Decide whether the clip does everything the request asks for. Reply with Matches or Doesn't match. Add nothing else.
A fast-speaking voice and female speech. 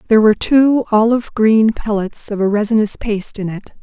Doesn't match